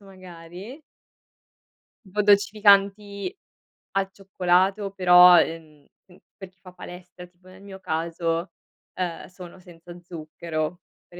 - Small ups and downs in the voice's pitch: Yes, narrow, 2.2 semitones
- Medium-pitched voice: Yes, medium, 180 Hz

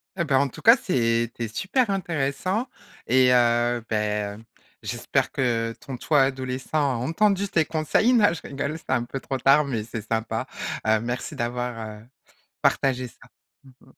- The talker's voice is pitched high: No, low, 130 Hz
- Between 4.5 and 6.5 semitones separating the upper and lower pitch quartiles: Yes, average, 4.9 semitones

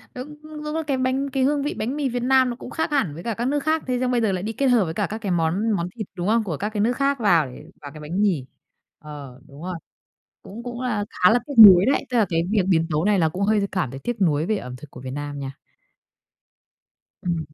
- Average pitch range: No, wide, 7.4 semitones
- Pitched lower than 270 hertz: Yes, high, 210 Hz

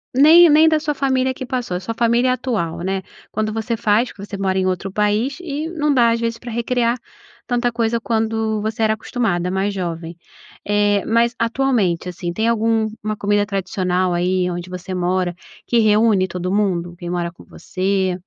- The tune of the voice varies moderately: Yes, average, 4.1 semitones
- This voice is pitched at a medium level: No, high, 215 Hz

